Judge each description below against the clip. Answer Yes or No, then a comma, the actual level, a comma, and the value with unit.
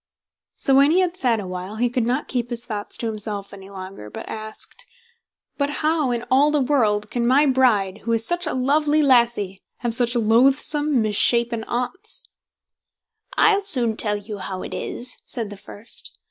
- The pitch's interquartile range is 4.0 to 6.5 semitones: Yes, average, 4.9 semitones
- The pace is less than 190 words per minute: Yes, average, 175 wpm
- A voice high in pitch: Yes, high, 240 Hz